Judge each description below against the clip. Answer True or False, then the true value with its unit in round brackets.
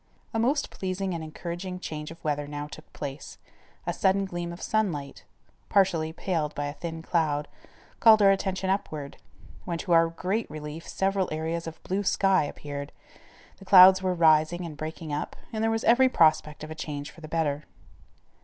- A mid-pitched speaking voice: True (165 Hz)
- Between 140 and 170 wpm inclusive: False (180 wpm)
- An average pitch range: True (3.8 semitones)